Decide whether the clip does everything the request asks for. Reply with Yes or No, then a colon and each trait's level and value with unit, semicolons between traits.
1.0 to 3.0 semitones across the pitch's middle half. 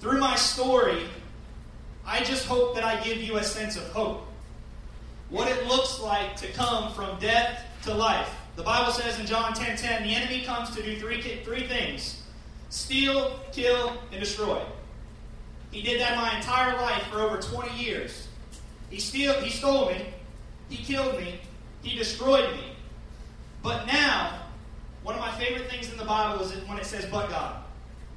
Yes: narrow, 2.6 semitones